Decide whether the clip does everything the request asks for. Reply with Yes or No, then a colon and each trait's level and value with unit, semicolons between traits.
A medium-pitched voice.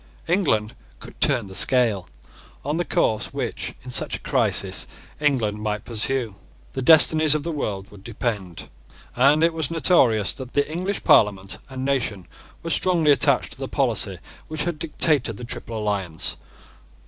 No: low, 130 Hz